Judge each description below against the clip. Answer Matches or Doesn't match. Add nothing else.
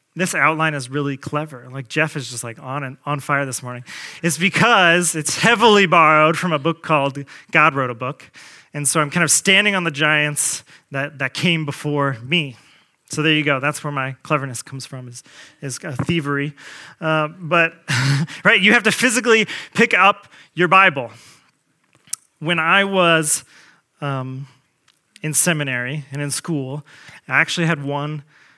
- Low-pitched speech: Doesn't match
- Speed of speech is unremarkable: Matches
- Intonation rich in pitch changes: Doesn't match